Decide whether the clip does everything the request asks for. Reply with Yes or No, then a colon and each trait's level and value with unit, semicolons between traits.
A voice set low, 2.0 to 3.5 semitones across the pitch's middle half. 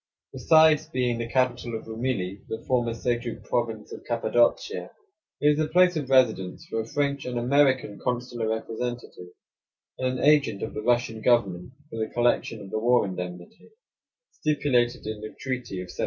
Yes: low, 120 Hz; average, 2.8 semitones